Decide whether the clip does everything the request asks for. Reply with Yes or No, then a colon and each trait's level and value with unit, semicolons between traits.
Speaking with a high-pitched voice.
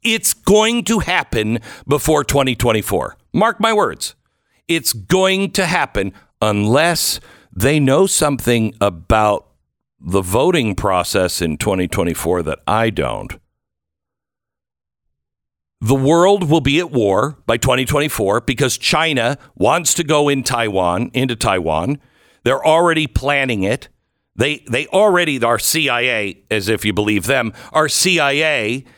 No: low, 130 Hz